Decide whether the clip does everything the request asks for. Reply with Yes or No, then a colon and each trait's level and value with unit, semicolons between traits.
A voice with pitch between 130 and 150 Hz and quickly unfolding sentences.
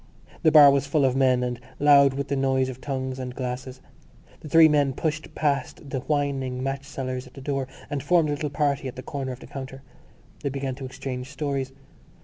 Yes: low, 135 Hz; fast, 210 wpm